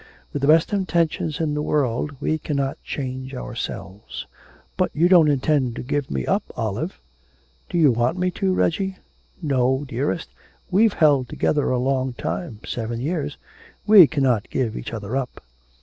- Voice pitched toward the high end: No, medium, 140 Hz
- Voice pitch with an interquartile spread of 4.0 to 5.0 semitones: Yes, average, 4.3 semitones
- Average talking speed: Yes, average, 160 wpm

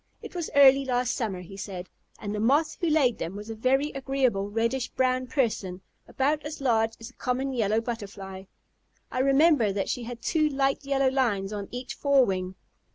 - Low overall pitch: No, high, 245 Hz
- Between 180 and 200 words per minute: Yes, average, 185 wpm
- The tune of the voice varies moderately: Yes, average, 4.7 semitones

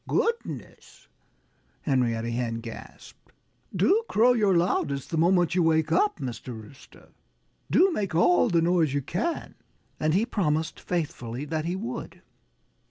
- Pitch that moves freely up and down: Yes, wide, 5.8 semitones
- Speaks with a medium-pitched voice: Yes, medium, 165 Hz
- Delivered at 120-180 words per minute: Yes, slow, 135 wpm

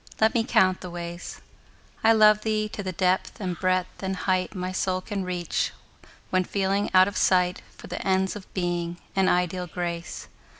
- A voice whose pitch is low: No, medium, 185 Hz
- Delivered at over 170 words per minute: Yes, average, 180 wpm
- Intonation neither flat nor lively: No, narrow, 1.7 semitones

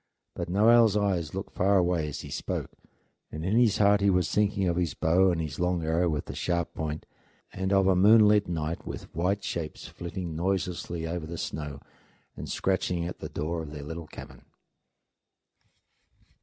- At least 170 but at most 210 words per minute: Yes, average, 180 wpm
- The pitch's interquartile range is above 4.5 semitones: No, average, 3.2 semitones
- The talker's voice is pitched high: No, very low, 90 Hz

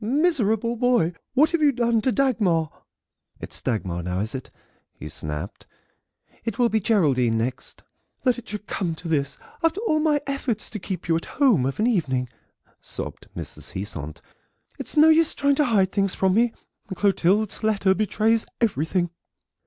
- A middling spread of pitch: No, wide, 7.5 semitones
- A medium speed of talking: Yes, average, 170 wpm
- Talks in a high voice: Yes, high, 210 Hz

